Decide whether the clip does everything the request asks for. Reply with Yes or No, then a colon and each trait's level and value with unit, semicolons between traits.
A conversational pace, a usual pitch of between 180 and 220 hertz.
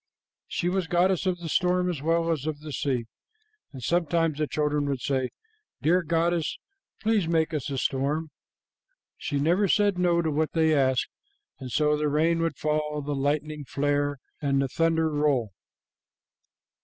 No: average, 165 wpm; medium, 155 Hz